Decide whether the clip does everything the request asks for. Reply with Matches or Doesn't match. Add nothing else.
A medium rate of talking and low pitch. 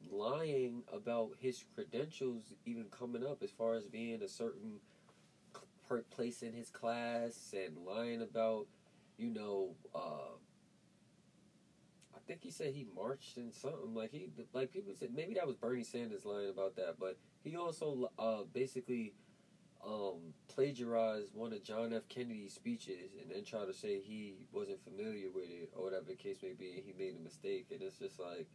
Matches